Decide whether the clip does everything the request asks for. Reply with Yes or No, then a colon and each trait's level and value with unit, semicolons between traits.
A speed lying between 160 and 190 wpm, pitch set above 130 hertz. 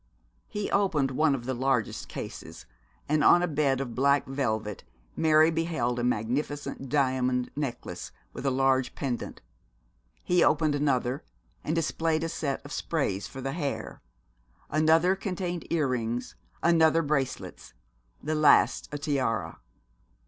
No: slow, 135 wpm; medium, 140 Hz